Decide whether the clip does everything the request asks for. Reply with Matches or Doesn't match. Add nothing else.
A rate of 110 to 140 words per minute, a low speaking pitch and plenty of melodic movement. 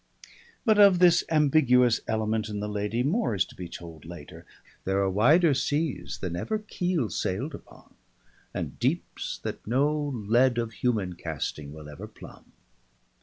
Doesn't match